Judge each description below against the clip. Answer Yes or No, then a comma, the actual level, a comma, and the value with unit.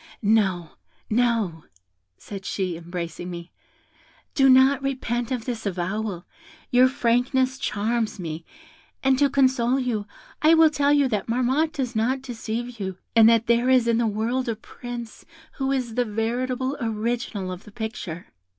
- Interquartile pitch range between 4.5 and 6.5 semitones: No, average, 3.7 semitones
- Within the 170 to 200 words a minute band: No, average, 150 wpm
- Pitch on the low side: No, high, 235 Hz